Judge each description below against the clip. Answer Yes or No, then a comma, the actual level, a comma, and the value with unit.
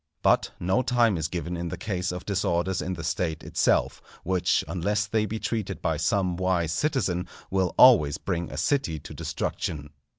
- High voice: No, very low, 90 Hz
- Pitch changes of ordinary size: Yes, average, 3.4 semitones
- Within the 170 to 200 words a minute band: Yes, average, 175 wpm